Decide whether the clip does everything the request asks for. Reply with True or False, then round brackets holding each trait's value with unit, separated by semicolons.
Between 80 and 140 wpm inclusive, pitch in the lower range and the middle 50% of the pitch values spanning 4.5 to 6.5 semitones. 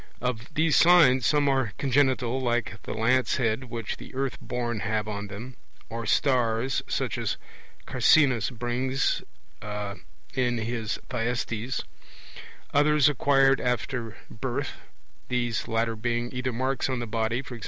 False (135 wpm; 120 Hz; 2.6 semitones)